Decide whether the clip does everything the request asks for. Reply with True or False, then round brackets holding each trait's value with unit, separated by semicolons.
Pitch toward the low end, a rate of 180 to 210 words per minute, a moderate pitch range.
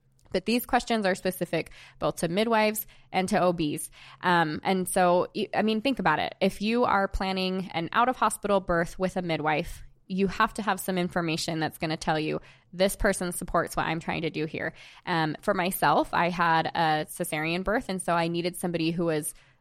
False (180 Hz; 200 wpm; 3.2 semitones)